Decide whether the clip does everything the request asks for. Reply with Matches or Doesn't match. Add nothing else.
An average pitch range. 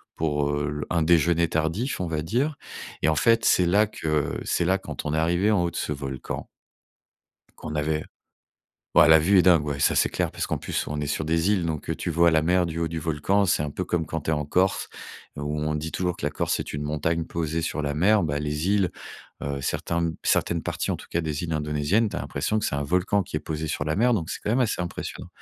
Matches